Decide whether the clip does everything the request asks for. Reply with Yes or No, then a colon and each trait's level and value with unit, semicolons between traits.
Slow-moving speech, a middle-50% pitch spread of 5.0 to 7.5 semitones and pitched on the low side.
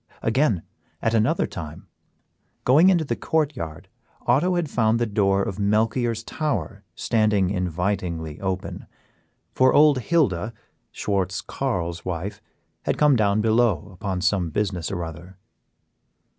Yes: slow, 130 wpm; average, 5.3 semitones; low, 105 Hz